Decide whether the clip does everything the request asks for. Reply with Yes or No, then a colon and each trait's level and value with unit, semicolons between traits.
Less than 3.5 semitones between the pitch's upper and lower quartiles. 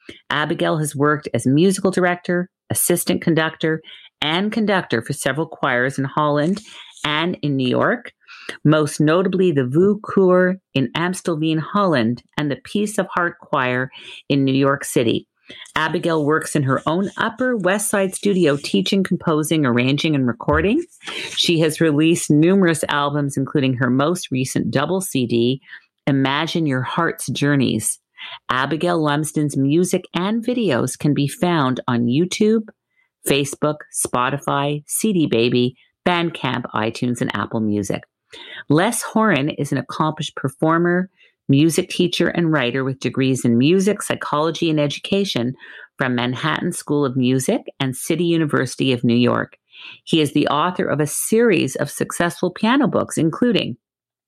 No: average, 4.8 semitones